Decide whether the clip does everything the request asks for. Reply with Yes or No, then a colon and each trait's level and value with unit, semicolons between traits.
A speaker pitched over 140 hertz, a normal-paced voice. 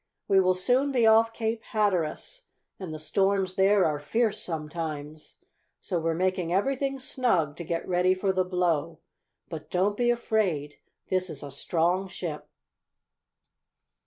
Yes: medium, 185 Hz; average, 145 wpm